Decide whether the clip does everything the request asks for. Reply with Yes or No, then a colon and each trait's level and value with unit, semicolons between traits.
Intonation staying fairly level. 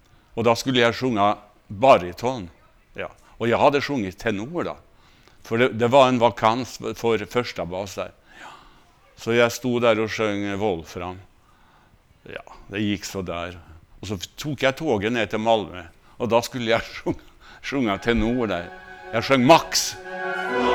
No: average, 3.4 semitones